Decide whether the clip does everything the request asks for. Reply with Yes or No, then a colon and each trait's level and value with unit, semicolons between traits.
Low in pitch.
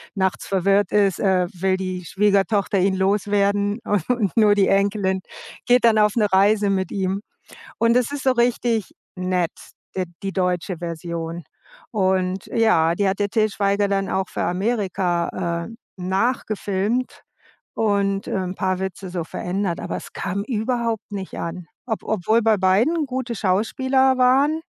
No: high, 200 Hz